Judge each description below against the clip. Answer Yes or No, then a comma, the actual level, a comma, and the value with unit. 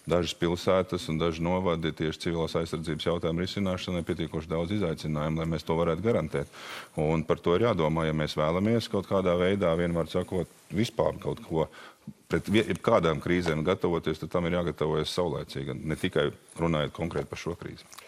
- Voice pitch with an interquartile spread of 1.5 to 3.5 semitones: Yes, narrow, 2.4 semitones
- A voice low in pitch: Yes, very low, 85 Hz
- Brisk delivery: No, average, 165 wpm